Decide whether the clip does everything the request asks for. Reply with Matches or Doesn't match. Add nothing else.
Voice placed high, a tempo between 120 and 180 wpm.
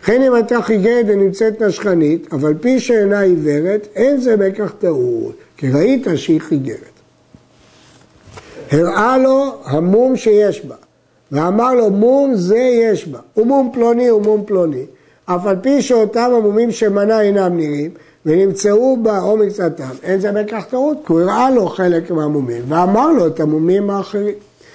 Matches